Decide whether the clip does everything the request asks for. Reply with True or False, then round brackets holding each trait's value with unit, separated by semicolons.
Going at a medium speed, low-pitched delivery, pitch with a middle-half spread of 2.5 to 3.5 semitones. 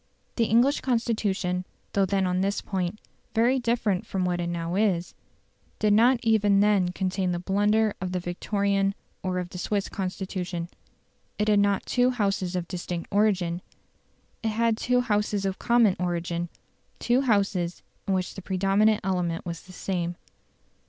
False (160 wpm; 195 Hz; 2.9 semitones)